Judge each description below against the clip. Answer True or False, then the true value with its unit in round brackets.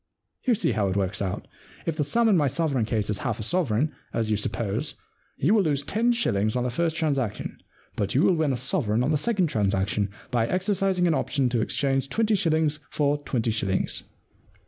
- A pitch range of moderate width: False (7.4 semitones)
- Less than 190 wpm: False (205 wpm)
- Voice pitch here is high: False (140 Hz)